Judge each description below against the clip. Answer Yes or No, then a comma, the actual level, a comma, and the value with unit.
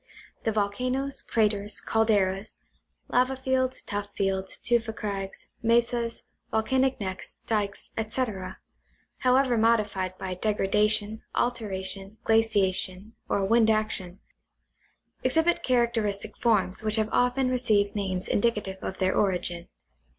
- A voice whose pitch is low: No, high, 215 Hz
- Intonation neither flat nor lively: Yes, average, 3.3 semitones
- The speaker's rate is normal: No, slow, 110 wpm